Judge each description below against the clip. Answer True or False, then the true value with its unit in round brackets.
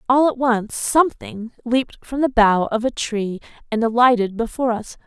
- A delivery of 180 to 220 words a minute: False (155 wpm)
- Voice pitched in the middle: False (235 Hz)